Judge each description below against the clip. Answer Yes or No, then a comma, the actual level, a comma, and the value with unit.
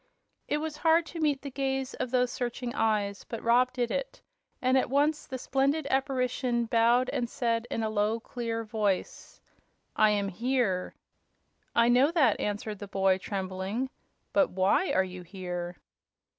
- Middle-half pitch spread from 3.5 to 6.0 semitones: Yes, average, 4.5 semitones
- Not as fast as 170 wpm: Yes, average, 160 wpm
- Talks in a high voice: Yes, high, 240 Hz